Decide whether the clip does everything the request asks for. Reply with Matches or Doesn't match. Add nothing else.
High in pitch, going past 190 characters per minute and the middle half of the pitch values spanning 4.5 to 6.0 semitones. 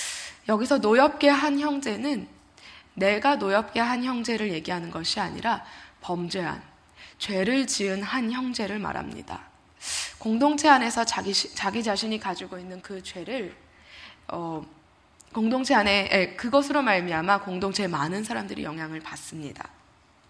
Matches